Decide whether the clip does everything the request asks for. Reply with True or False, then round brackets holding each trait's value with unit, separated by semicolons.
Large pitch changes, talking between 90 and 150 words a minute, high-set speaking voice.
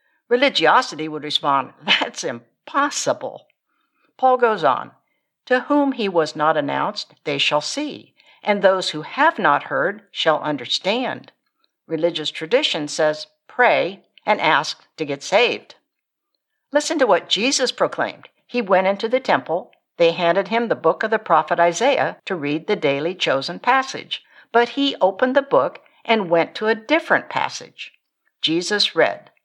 True (8.1 semitones; 145 wpm; 205 Hz)